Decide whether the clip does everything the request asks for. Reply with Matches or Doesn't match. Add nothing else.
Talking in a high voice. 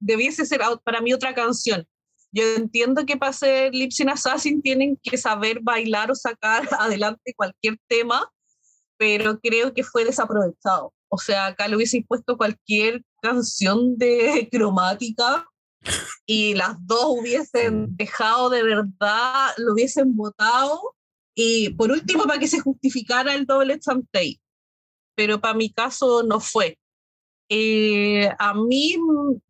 Matches